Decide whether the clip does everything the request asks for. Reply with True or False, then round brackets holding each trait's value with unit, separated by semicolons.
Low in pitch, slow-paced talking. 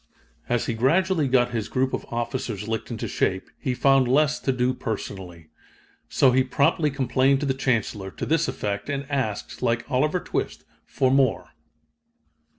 False (130 Hz; 160 wpm)